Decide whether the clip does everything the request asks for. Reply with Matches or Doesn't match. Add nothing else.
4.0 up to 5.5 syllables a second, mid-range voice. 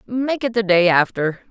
Doesn't match